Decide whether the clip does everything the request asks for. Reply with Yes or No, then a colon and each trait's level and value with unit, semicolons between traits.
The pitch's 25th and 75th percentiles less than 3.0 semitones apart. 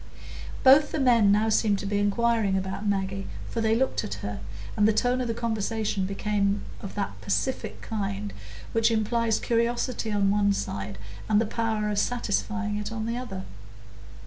Yes: narrow, 2.4 semitones